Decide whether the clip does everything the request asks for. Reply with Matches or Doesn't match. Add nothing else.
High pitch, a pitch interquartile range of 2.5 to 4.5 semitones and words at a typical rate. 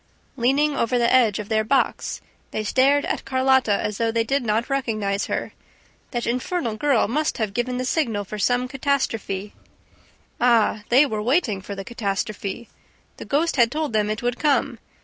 Matches